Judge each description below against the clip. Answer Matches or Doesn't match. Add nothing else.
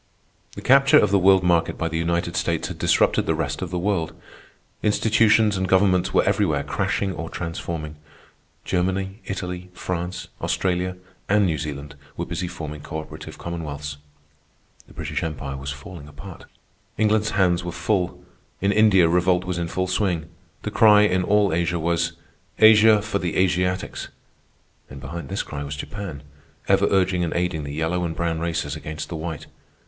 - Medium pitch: Doesn't match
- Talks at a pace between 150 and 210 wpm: Matches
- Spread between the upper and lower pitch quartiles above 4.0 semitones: Doesn't match